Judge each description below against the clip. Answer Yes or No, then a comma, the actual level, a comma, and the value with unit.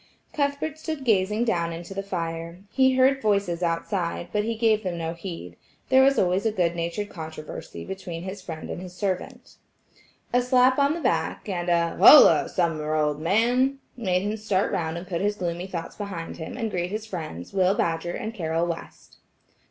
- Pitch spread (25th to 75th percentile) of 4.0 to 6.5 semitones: Yes, average, 4.6 semitones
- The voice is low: No, medium, 185 Hz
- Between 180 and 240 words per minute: Yes, average, 185 wpm